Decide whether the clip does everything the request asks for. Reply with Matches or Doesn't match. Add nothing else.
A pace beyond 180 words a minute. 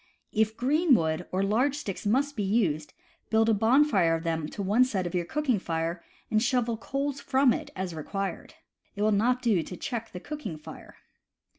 Matches